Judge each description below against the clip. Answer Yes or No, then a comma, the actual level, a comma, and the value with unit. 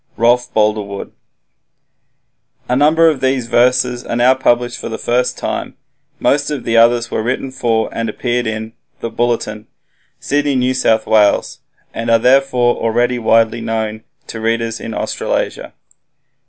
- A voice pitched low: Yes, low, 120 Hz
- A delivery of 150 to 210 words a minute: No, average, 140 wpm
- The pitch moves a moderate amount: No, narrow, 2.0 semitones